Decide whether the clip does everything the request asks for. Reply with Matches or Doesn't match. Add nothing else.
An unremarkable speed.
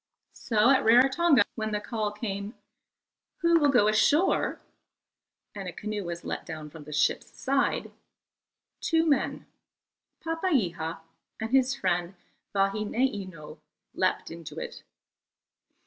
Doesn't match